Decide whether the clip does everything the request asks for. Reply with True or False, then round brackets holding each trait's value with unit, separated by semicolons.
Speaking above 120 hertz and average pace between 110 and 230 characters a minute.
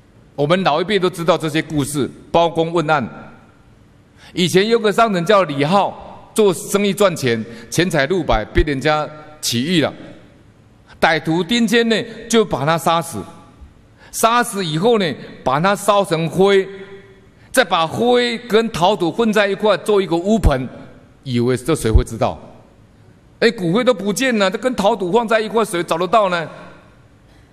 True (185 Hz; 220 characters per minute)